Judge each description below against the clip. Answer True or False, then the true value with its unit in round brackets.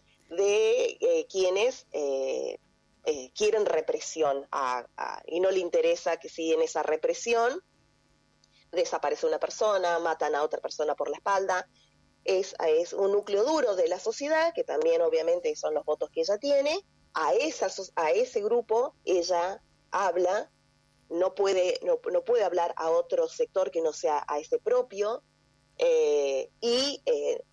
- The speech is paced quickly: False (155 wpm)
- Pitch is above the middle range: True (390 Hz)